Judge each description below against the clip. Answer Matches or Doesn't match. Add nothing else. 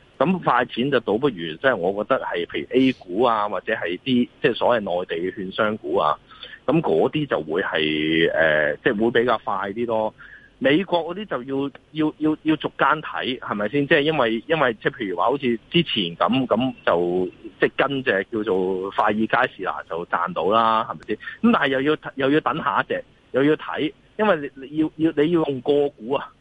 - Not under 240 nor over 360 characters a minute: Matches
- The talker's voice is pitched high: Doesn't match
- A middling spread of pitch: Doesn't match